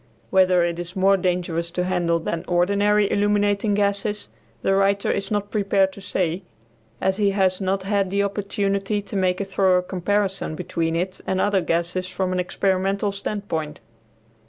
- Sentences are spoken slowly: No, average, 160 wpm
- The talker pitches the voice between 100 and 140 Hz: No, high, 190 Hz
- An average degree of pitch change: No, narrow, 1.8 semitones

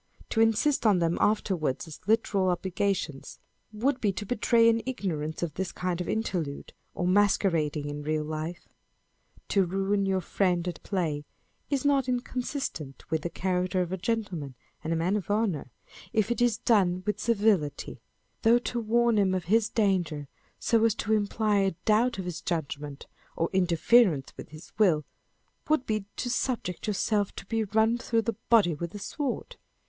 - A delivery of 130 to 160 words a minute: No, average, 170 wpm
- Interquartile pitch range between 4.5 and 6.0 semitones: Yes, average, 4.8 semitones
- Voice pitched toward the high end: Yes, high, 195 Hz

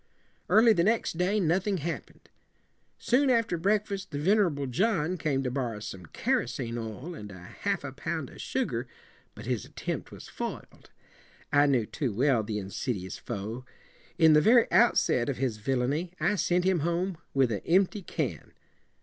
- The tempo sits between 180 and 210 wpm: Yes, fast, 205 wpm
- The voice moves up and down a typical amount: No, wide, 7.6 semitones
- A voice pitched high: No, medium, 150 Hz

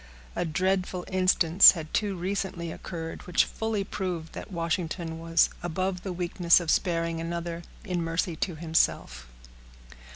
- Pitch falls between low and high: Yes, medium, 170 Hz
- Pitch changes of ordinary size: No, narrow, 2.0 semitones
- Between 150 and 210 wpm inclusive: No, slow, 135 wpm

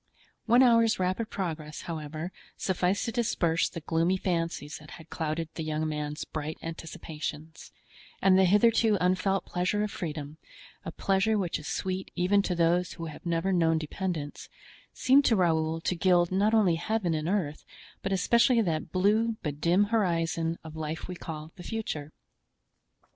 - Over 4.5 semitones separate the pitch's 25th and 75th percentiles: No, average, 3.6 semitones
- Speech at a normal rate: Yes, average, 155 wpm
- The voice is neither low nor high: Yes, medium, 175 Hz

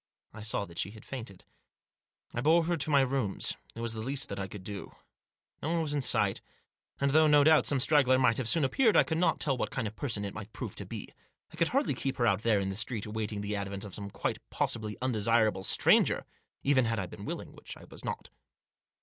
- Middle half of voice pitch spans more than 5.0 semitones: Yes, wide, 5.4 semitones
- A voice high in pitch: No, low, 115 Hz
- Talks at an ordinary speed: No, fast, 240 wpm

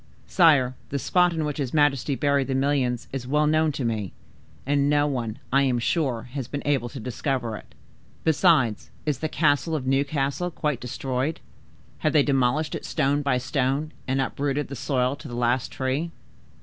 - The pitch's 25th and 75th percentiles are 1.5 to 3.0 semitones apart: Yes, narrow, 2.6 semitones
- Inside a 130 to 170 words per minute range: No, average, 180 wpm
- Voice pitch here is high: No, medium, 140 Hz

